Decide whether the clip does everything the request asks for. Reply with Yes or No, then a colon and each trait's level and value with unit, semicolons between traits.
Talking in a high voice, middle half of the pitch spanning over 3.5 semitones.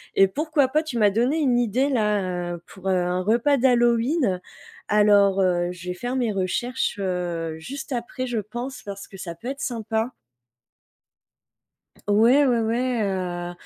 Yes: high, 220 Hz; average, 5.2 semitones